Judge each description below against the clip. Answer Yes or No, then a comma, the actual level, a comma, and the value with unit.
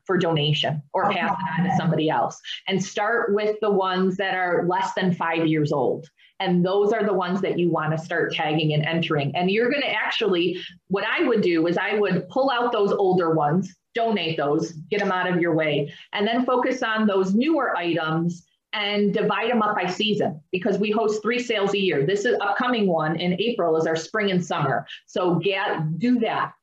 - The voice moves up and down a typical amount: Yes, average, 4.1 semitones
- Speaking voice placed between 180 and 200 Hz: Yes, medium, 185 Hz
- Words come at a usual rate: No, fast, 210 wpm